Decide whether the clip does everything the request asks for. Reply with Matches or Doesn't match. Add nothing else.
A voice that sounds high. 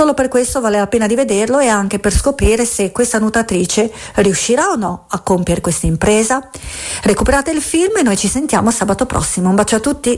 Matches